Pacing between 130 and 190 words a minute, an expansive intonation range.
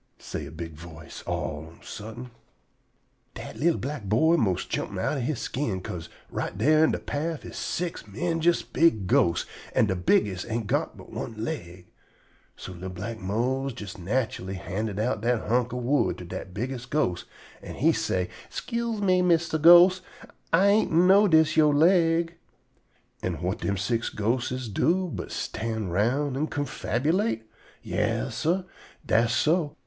Yes: average, 160 wpm; wide, 8.1 semitones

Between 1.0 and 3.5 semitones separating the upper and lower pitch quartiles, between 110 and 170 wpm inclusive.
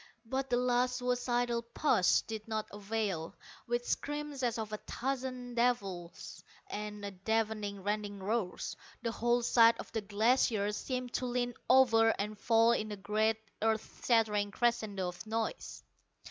Yes: average, 2.7 semitones; average, 145 wpm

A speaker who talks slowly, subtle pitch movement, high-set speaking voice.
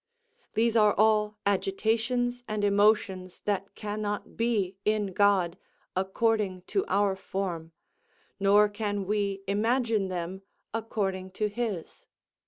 Yes: slow, 110 wpm; narrow, 2.1 semitones; high, 205 Hz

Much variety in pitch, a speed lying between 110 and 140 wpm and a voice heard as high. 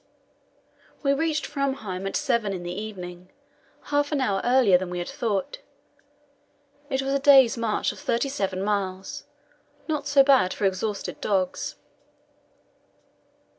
Yes: wide, 6.5 semitones; slow, 135 wpm; high, 220 Hz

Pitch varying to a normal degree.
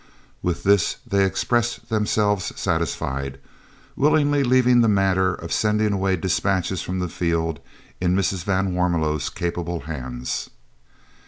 Yes: average, 3.6 semitones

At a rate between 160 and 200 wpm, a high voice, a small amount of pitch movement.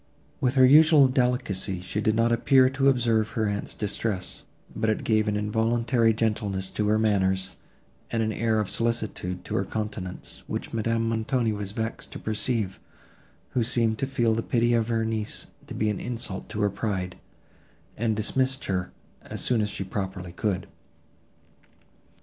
No: average, 165 wpm; low, 110 Hz; narrow, 2.3 semitones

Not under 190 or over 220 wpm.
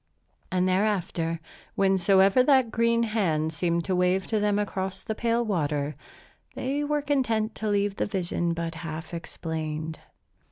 No: average, 145 wpm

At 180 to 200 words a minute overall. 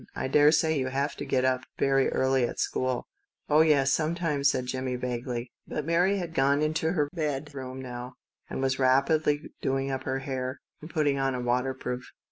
Yes: average, 190 wpm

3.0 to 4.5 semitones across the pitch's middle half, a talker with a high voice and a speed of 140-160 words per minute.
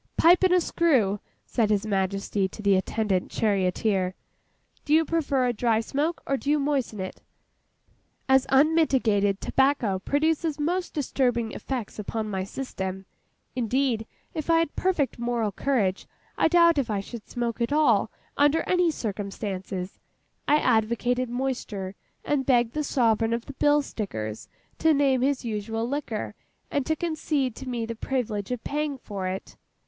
No: wide, 5.6 semitones; high, 245 Hz; average, 155 wpm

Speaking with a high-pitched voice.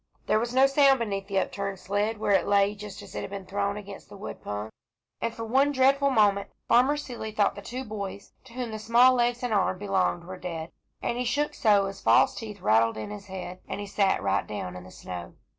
Yes: high, 205 Hz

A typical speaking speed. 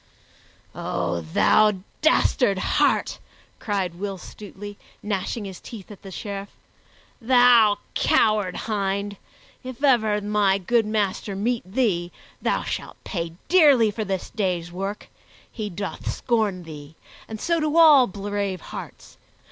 No: slow, 125 wpm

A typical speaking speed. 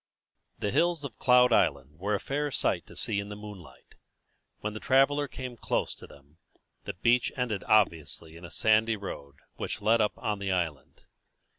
Yes: average, 180 wpm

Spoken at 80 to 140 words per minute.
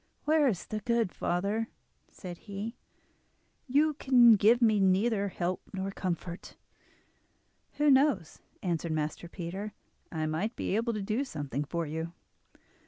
Yes: slow, 135 wpm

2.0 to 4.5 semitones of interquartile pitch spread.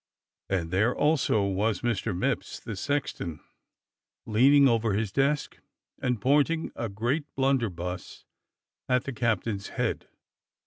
No: wide, 5.5 semitones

